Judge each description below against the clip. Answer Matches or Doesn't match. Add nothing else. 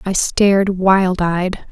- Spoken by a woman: Matches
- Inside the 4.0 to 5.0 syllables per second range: Doesn't match